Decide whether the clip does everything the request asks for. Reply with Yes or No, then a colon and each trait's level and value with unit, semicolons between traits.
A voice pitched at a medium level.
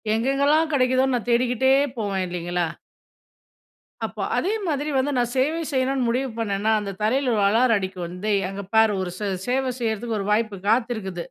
No: high, 230 Hz